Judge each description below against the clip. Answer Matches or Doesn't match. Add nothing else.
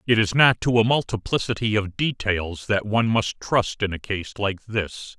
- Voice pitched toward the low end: Matches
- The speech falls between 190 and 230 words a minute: Matches